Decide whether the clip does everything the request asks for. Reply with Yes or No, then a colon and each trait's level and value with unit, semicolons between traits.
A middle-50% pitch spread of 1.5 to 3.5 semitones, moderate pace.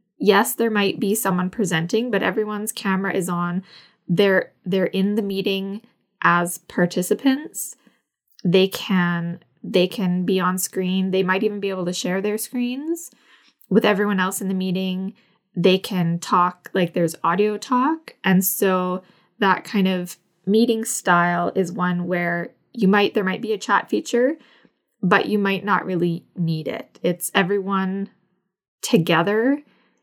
Yes: narrow, 2.6 semitones; average, 150 wpm